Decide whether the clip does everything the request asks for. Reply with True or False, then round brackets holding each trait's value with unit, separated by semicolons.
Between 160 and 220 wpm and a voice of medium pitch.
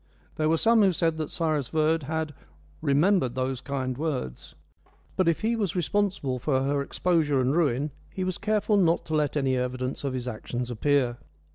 True (180 wpm; 150 Hz)